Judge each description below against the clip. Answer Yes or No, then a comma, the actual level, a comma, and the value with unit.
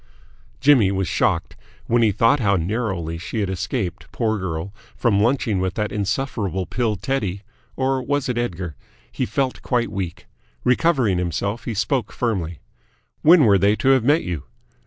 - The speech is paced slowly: No, average, 160 wpm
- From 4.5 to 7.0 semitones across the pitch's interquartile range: Yes, average, 4.8 semitones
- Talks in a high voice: No, low, 105 Hz